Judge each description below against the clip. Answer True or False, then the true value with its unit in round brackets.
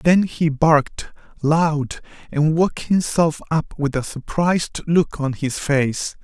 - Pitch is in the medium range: True (155 Hz)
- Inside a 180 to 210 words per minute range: False (145 wpm)